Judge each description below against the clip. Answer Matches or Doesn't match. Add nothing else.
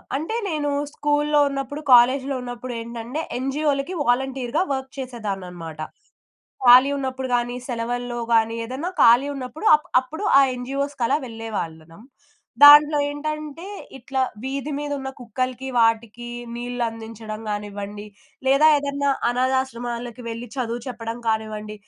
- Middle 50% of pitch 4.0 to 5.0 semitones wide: Doesn't match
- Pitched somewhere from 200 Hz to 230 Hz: Doesn't match